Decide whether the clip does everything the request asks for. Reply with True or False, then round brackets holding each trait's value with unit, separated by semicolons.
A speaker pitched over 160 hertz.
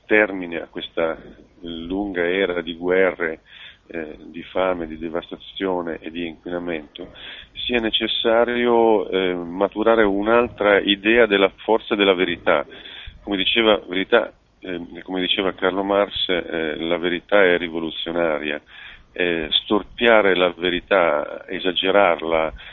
False (95 Hz)